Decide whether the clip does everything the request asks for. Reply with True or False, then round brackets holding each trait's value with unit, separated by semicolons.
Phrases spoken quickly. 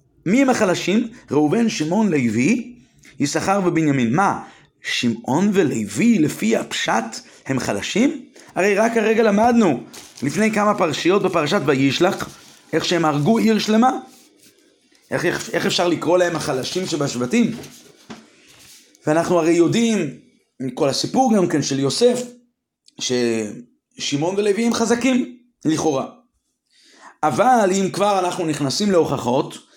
False (115 wpm)